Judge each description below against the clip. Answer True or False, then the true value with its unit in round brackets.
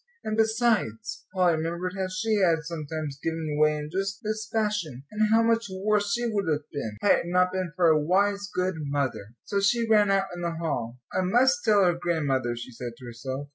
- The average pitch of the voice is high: False (180 Hz)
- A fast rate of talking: True (210 wpm)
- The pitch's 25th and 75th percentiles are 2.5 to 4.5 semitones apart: False (5.4 semitones)